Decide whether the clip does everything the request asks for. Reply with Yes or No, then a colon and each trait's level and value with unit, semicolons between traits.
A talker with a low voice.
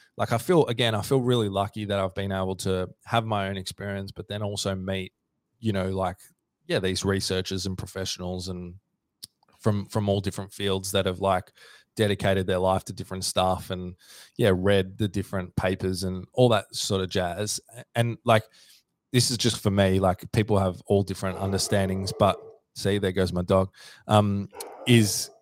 Yes: very low, 95 Hz